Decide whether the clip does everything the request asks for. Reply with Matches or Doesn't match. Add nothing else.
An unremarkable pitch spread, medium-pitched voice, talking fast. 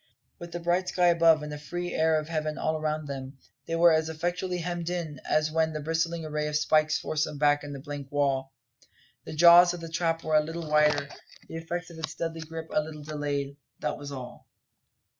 Doesn't match